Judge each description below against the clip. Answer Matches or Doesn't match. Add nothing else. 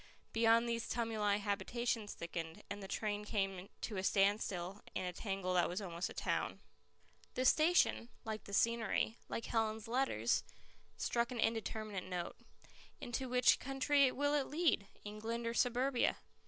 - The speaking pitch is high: Matches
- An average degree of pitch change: Matches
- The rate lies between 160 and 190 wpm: Doesn't match